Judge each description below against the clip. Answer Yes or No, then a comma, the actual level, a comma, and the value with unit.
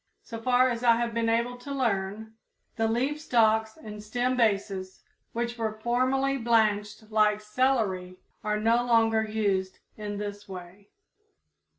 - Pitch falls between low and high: No, high, 220 Hz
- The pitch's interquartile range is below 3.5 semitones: Yes, narrow, 2.4 semitones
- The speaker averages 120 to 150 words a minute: Yes, average, 145 wpm